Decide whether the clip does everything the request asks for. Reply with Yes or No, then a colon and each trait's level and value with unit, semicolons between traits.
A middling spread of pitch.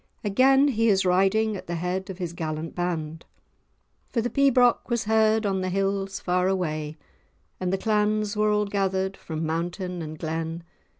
Yes: average, 3.7 semitones